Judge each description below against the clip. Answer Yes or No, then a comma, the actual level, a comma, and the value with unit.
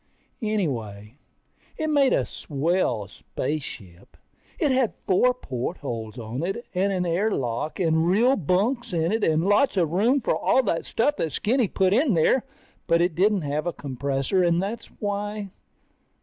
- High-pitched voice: No, medium, 180 Hz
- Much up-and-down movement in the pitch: Yes, wide, 6.8 semitones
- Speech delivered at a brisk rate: No, average, 160 wpm